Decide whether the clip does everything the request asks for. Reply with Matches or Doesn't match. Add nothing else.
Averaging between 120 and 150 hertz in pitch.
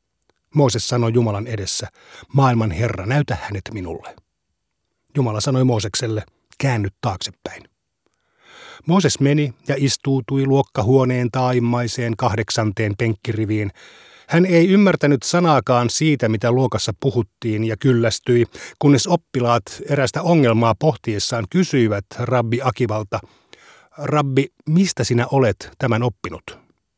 Matches